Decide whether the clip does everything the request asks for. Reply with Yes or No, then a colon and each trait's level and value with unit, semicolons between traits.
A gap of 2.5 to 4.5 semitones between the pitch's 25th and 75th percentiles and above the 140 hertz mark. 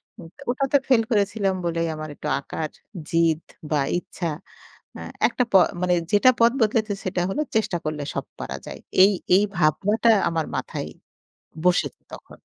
No: average, 5.0 semitones; high, 190 Hz